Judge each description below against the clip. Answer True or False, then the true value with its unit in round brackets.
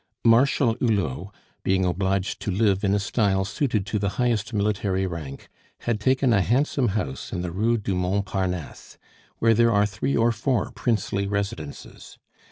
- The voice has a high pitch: False (100 Hz)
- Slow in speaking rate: False (165 wpm)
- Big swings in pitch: False (3.2 semitones)